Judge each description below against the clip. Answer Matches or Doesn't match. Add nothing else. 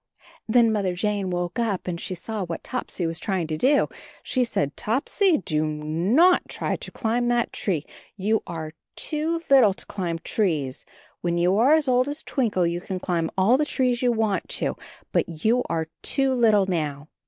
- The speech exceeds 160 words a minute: Matches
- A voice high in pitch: Matches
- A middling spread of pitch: Doesn't match